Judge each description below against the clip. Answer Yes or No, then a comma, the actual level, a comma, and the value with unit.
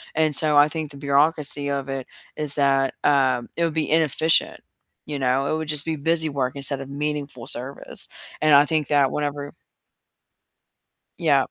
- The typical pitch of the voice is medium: Yes, medium, 145 Hz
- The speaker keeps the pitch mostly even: Yes, narrow, 1.9 semitones